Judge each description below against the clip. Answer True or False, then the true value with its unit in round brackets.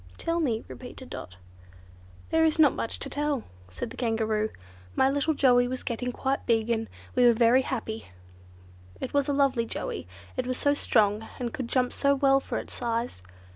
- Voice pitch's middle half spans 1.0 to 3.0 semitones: False (3.4 semitones)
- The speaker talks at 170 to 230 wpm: True (185 wpm)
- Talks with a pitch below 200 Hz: False (250 Hz)